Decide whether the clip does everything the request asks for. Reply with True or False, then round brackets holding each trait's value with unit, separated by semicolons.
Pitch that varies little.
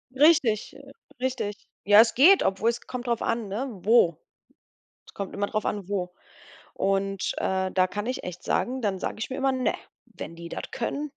False (4.5 semitones)